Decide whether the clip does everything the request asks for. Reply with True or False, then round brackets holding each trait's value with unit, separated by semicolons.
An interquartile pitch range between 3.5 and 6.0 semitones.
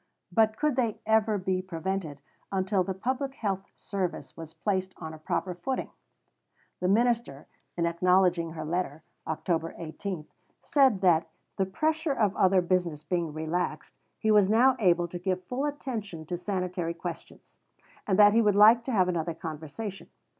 True (4.2 semitones)